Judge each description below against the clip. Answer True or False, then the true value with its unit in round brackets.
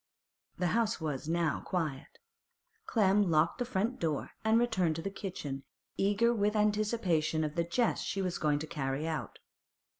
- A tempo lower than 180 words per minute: True (160 wpm)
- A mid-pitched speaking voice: True (175 Hz)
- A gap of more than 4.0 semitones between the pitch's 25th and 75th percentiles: True (5.2 semitones)